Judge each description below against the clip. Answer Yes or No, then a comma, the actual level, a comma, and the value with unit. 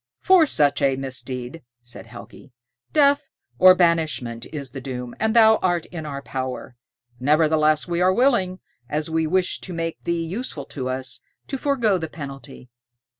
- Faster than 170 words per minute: No, average, 160 wpm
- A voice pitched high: No, medium, 155 Hz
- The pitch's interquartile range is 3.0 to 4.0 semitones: No, wide, 5.6 semitones